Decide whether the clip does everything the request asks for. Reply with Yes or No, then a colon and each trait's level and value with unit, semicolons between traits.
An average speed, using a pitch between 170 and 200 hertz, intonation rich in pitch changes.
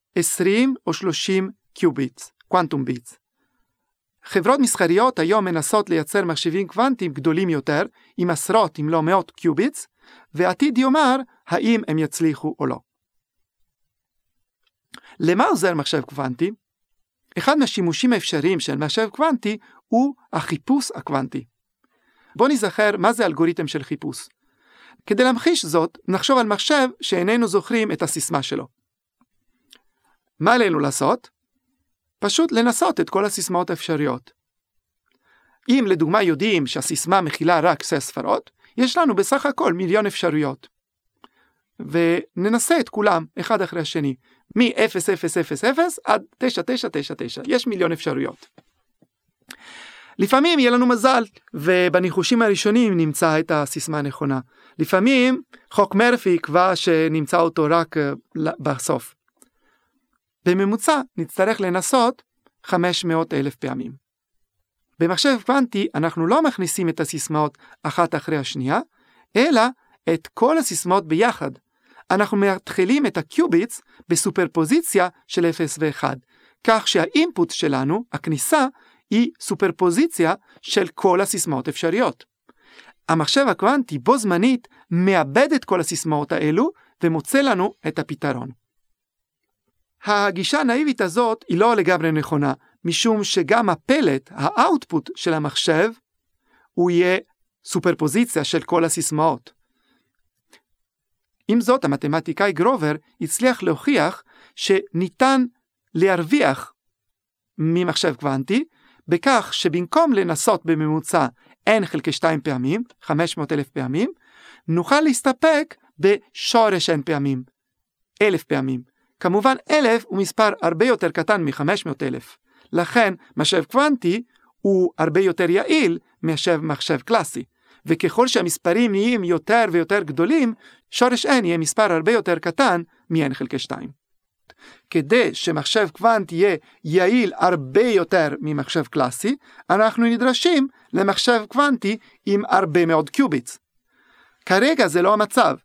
Yes: average, 110 wpm; medium, 185 Hz; wide, 6.6 semitones